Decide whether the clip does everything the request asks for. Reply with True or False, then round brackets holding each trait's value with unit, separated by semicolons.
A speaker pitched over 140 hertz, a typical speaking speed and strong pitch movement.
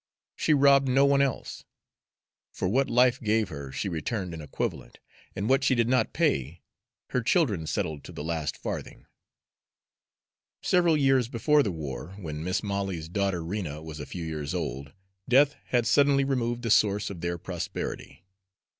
False (100 Hz; 165 wpm; 8.2 semitones)